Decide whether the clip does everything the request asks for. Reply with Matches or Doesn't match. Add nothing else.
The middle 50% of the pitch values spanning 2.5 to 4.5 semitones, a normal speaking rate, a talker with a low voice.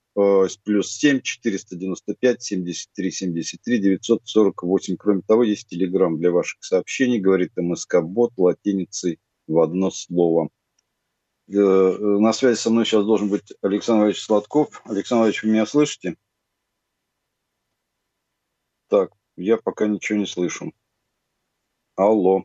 Matches